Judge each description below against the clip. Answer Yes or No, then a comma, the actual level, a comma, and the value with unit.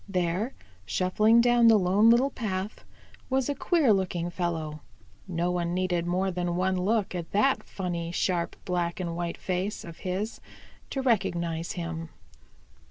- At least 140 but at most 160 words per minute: Yes, average, 150 wpm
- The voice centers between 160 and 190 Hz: Yes, medium, 185 Hz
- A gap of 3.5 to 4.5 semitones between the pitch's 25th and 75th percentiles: Yes, average, 3.8 semitones